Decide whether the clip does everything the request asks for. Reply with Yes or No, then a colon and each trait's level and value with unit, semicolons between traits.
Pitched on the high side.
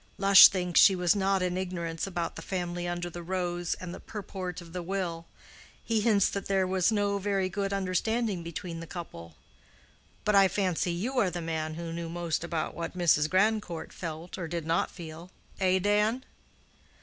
No: medium, 180 Hz